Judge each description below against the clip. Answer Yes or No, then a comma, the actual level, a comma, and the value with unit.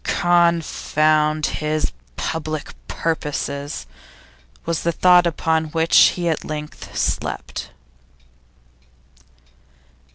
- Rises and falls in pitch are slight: Yes, narrow, 1.6 semitones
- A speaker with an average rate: No, slow, 75 wpm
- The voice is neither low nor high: Yes, medium, 160 Hz